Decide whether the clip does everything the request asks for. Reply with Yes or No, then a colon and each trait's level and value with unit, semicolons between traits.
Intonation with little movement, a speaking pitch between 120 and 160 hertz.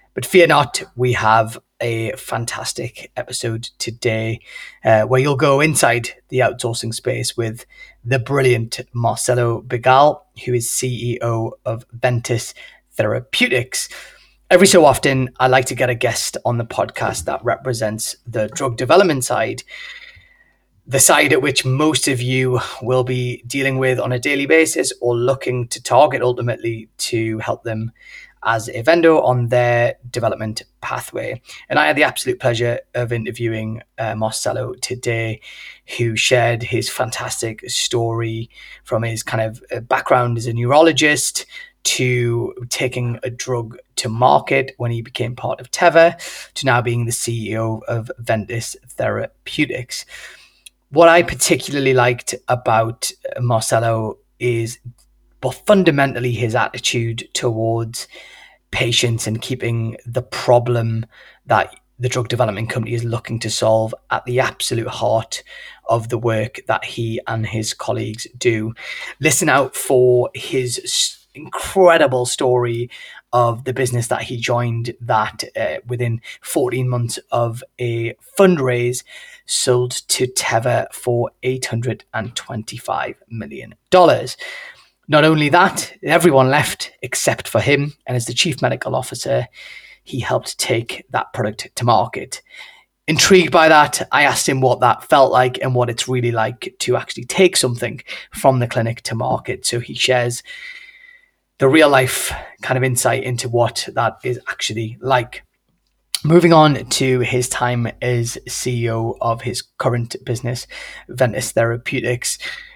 Yes: narrow, 2.0 semitones; low, 125 Hz